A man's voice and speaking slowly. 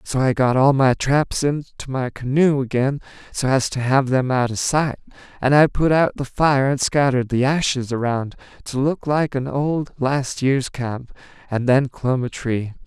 No: male; average, 195 wpm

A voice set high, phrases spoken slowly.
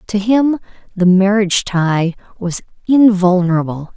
Yes: high, 195 Hz; slow, 105 wpm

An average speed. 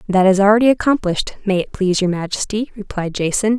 Yes: average, 185 wpm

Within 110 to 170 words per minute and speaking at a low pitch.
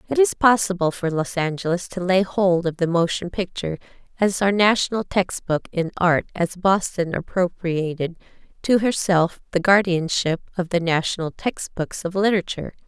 No: average, 160 wpm; medium, 180 Hz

